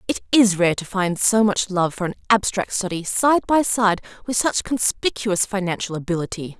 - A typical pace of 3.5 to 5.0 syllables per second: Yes, 4.9 syllables/s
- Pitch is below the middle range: No, high, 200 Hz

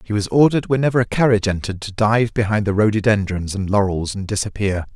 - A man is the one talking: Yes, male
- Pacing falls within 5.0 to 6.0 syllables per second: No, 6.5 syllables/s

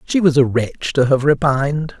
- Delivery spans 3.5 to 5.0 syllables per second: Yes, 4.8 syllables/s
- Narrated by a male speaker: Yes, male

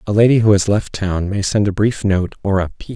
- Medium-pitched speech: No, low, 100 Hz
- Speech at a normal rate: No, fast, 285 wpm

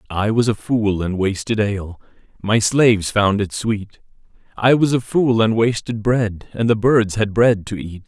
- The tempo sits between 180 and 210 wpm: Yes, average, 195 wpm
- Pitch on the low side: Yes, low, 110 Hz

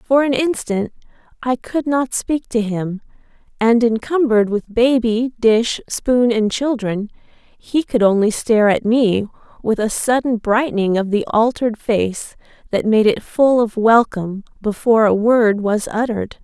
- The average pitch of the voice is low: No, high, 230 Hz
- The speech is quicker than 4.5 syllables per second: No, 4.4 syllables/s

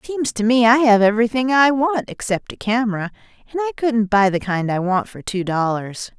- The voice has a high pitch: Yes, high, 225 Hz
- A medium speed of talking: No, fast, 215 wpm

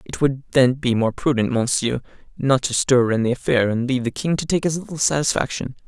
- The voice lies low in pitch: Yes, low, 130 Hz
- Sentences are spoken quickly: Yes, fast, 225 wpm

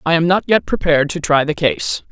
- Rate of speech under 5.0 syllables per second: No, 5.7 syllables/s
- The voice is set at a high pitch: No, medium, 165 Hz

